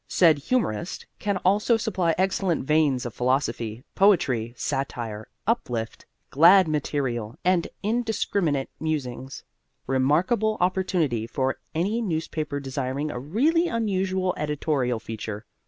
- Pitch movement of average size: No, wide, 6.8 semitones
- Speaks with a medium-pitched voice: Yes, medium, 155 Hz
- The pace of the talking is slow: Yes, slow, 105 wpm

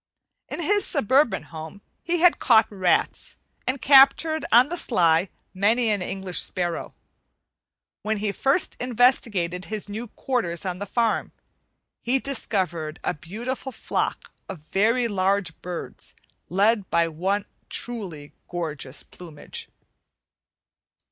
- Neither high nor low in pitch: No, high, 205 Hz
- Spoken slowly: Yes, slow, 120 wpm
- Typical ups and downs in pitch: No, wide, 5.7 semitones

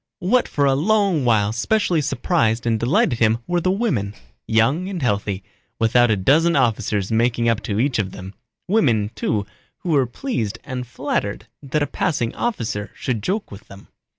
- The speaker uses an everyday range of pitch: No, wide, 6.6 semitones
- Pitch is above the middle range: No, low, 120 Hz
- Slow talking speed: No, average, 175 wpm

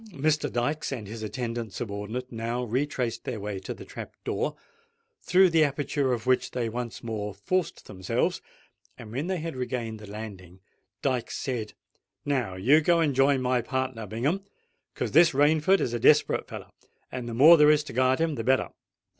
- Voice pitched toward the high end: No, low, 125 Hz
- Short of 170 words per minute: No, average, 180 wpm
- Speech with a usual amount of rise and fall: Yes, average, 4.6 semitones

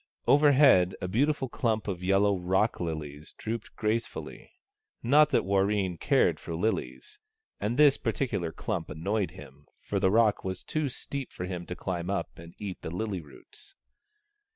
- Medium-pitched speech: No, low, 100 Hz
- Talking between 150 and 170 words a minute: Yes, average, 160 wpm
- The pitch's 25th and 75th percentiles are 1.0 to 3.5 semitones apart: No, average, 4.7 semitones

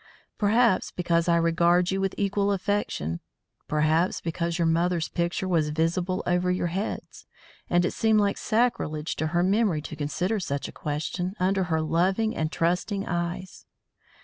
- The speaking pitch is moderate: Yes, medium, 175 Hz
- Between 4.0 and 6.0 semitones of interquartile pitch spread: No, average, 2.8 semitones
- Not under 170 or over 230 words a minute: No, average, 155 wpm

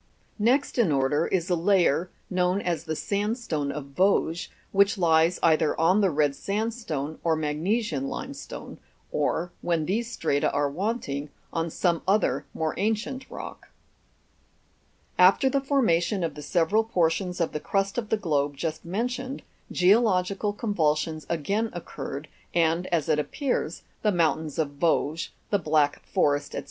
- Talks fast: No, average, 145 wpm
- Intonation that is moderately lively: Yes, average, 4.8 semitones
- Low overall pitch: No, medium, 175 Hz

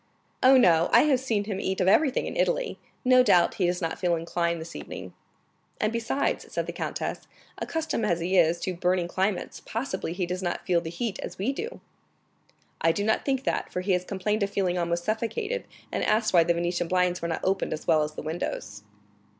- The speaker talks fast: Yes, fast, 215 wpm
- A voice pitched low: No, medium, 185 Hz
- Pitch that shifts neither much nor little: Yes, average, 4.7 semitones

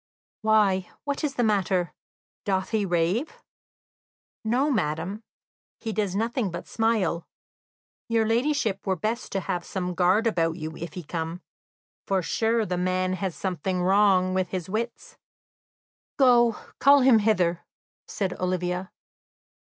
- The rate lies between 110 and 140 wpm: Yes, slow, 135 wpm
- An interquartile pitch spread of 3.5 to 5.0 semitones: Yes, average, 3.9 semitones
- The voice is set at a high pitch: Yes, high, 195 Hz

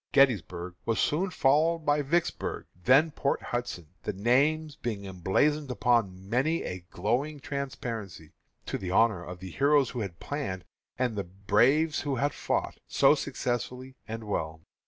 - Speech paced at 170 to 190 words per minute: No, average, 150 wpm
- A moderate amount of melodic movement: No, wide, 6.8 semitones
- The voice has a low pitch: Yes, low, 120 Hz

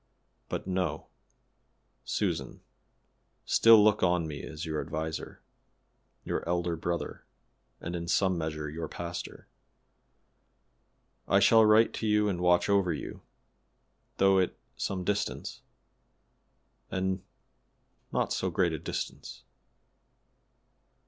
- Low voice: Yes, very low, 90 Hz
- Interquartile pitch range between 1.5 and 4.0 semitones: Yes, average, 3.1 semitones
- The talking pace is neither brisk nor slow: No, slow, 110 wpm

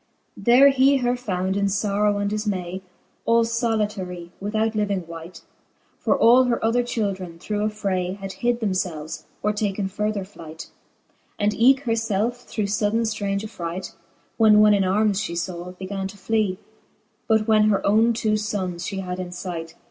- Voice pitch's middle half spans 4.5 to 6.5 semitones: No, average, 3.0 semitones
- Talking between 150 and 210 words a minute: Yes, average, 165 wpm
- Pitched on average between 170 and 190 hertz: No, high, 205 Hz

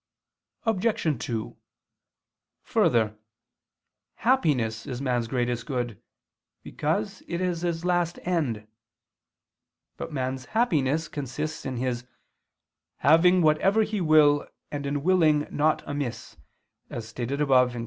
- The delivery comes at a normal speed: No, slow, 110 wpm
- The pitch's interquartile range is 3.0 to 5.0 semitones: No, wide, 5.6 semitones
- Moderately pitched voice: Yes, medium, 145 Hz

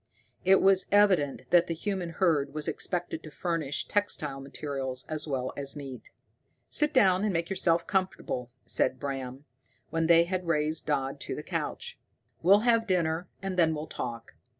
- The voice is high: No, medium, 165 Hz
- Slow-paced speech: No, average, 165 wpm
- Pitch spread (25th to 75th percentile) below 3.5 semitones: No, average, 4.8 semitones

